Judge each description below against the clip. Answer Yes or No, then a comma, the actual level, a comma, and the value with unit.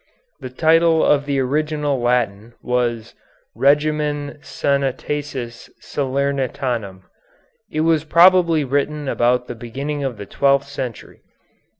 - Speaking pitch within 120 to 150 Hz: Yes, medium, 140 Hz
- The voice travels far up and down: No, average, 3.1 semitones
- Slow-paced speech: Yes, slow, 105 wpm